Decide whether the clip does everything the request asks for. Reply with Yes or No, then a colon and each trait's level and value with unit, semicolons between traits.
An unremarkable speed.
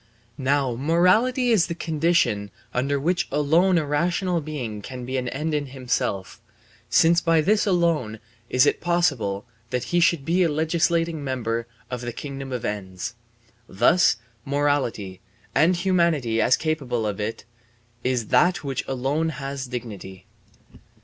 Yes: average, 145 wpm